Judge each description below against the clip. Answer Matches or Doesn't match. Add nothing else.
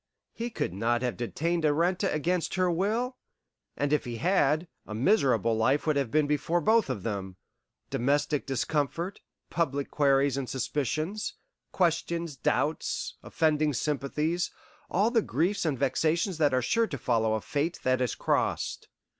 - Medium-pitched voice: Matches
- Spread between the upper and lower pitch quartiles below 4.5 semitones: Doesn't match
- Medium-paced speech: Matches